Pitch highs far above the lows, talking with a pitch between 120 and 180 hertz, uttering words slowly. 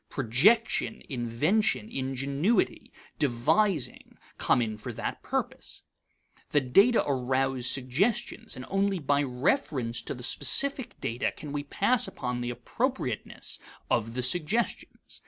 Yes: wide, 7.9 semitones; medium, 140 Hz; slow, 120 wpm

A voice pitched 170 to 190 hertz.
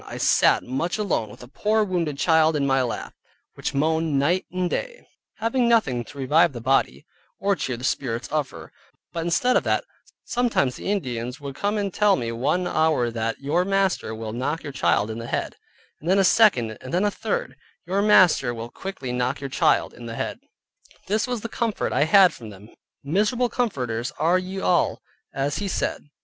No: medium, 155 Hz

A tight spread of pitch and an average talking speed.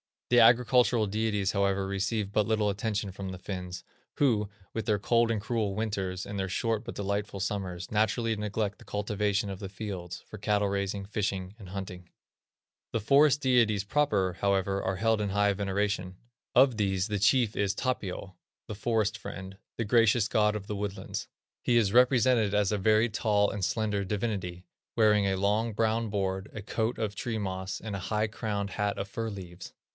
Yes: narrow, 2.2 semitones; average, 180 wpm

